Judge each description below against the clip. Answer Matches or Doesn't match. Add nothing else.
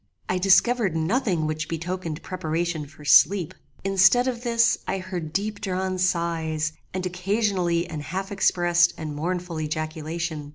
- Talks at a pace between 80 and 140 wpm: Matches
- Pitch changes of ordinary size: Matches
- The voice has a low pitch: Doesn't match